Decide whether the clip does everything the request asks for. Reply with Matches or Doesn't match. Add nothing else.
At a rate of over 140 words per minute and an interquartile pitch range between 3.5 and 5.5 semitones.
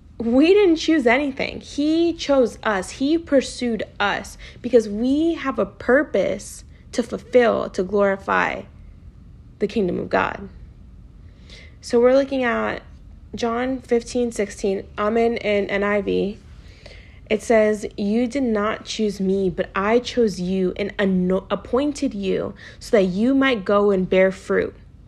Doesn't match